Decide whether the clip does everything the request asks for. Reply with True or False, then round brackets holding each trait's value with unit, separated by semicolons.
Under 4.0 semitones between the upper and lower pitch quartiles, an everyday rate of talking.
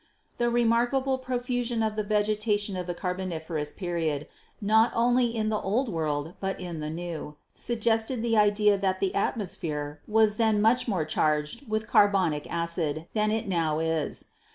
False (5.2 semitones; 160 wpm)